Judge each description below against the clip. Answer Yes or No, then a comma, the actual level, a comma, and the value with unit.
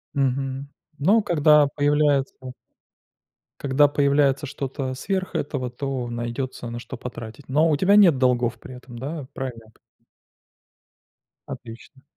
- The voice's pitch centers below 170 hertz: Yes, low, 135 Hz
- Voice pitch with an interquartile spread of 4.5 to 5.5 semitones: No, average, 2.8 semitones